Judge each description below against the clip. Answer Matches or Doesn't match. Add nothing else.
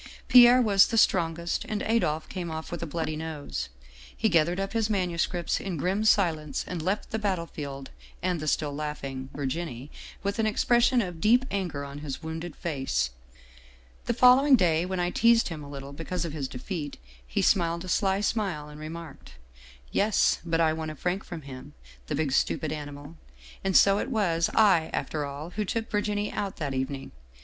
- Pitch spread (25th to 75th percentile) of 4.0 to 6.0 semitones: Matches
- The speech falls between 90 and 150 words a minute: Doesn't match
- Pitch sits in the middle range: Matches